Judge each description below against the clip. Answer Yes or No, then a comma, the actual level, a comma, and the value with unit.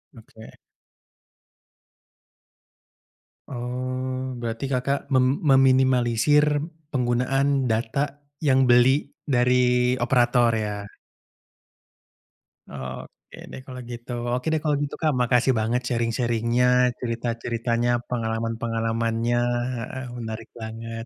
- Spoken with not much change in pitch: Yes, narrow, 2.2 semitones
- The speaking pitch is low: Yes, low, 125 Hz